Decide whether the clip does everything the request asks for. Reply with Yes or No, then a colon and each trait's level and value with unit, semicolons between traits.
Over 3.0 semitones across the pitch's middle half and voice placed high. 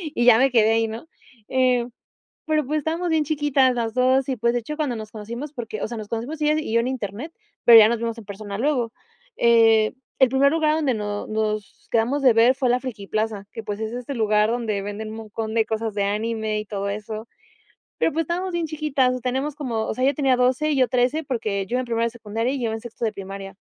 Yes: average, 3.5 semitones; high, 235 Hz